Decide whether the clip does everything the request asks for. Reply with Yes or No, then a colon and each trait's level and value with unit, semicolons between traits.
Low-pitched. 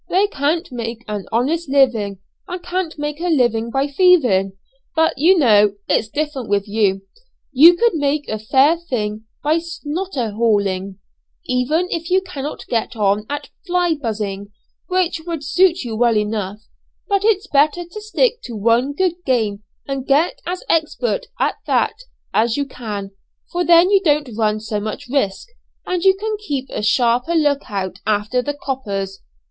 No: very high, 275 Hz